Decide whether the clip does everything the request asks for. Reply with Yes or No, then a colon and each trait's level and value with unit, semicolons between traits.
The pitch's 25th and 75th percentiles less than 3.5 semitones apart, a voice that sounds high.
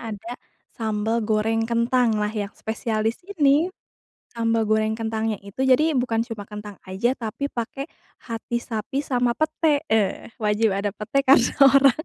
Yes: average, 2.9 semitones; high, 225 Hz